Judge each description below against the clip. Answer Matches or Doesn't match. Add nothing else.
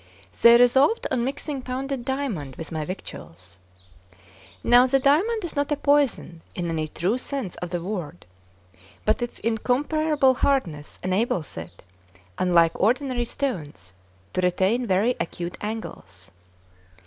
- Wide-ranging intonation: Matches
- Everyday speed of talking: Doesn't match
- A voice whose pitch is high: Matches